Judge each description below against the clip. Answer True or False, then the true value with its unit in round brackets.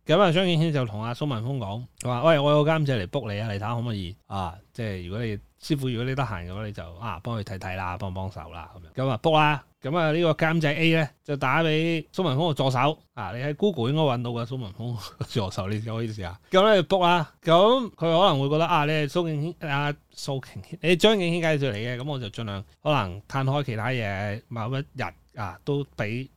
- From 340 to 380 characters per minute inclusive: True (360 characters per minute)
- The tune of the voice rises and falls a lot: True (6.4 semitones)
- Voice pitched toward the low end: True (130 Hz)